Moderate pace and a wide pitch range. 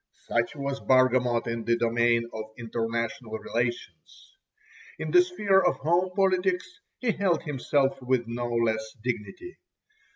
No: slow, 130 wpm; wide, 6.8 semitones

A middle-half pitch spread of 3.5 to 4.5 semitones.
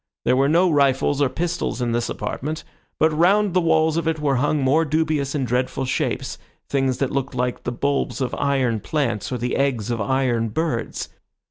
Yes: average, 3.9 semitones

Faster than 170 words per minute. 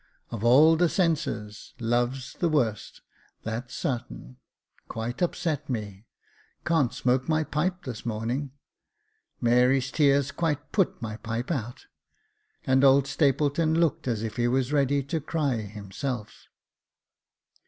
No: average, 140 wpm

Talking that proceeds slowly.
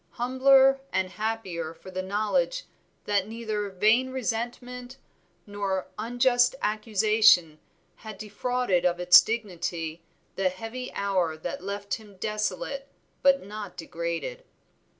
Yes: slow, 110 wpm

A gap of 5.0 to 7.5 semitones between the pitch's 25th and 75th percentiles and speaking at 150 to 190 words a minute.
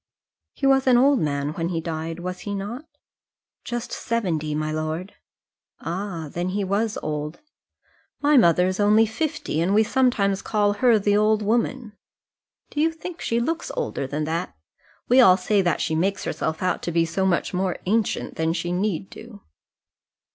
Yes: wide, 5.5 semitones; average, 175 wpm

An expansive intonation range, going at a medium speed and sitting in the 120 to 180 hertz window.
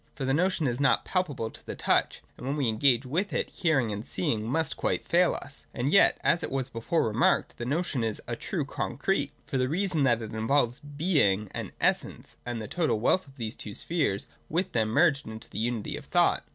No: wide, 6.0 semitones; fast, 225 wpm; low, 135 Hz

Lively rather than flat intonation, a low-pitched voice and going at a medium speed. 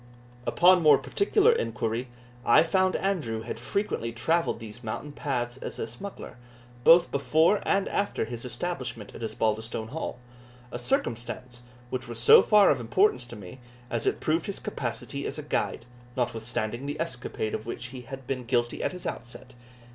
Yes: wide, 5.9 semitones; low, 125 Hz; average, 165 wpm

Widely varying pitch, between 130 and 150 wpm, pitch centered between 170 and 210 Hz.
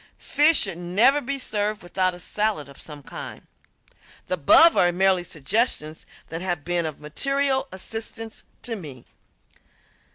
Yes: wide, 5.7 semitones; average, 140 wpm; medium, 185 Hz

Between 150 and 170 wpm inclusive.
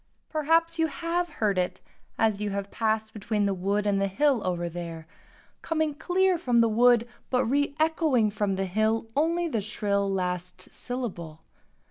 Yes: average, 160 wpm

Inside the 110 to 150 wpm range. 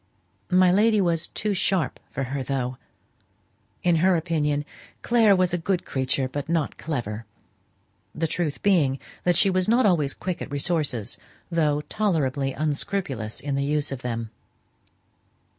Yes: average, 145 wpm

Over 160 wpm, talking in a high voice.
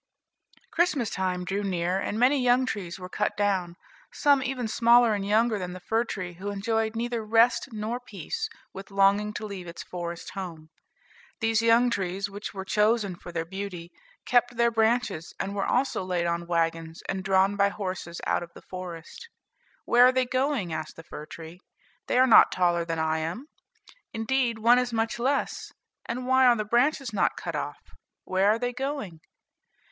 Yes: average, 180 wpm; high, 205 Hz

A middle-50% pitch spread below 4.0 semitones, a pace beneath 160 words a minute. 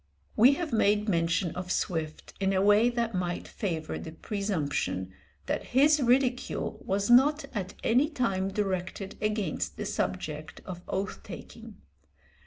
No: average, 4.7 semitones; average, 140 wpm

